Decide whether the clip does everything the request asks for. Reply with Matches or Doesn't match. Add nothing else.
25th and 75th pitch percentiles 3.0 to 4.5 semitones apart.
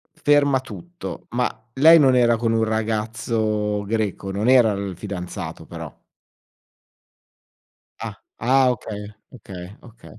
Matches